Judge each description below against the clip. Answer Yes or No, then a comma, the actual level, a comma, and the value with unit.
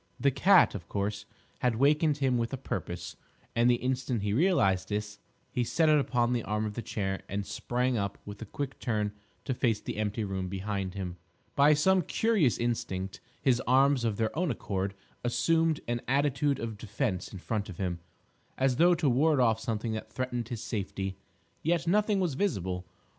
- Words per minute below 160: No, average, 185 wpm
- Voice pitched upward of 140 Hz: No, low, 120 Hz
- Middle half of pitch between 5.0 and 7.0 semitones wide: Yes, wide, 5.5 semitones